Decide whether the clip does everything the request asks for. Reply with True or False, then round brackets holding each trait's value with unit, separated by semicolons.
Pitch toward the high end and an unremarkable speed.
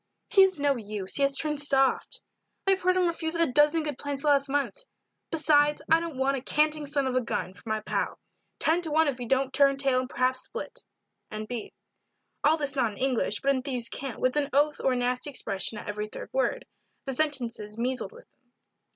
False (275 Hz; 225 wpm)